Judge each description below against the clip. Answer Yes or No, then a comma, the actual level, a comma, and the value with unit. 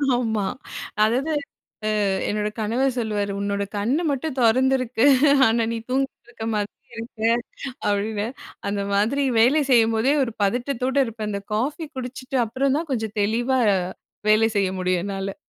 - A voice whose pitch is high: Yes, high, 230 Hz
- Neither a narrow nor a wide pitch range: Yes, average, 3.8 semitones